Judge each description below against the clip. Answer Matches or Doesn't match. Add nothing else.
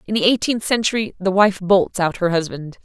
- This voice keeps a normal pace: Doesn't match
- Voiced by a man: Doesn't match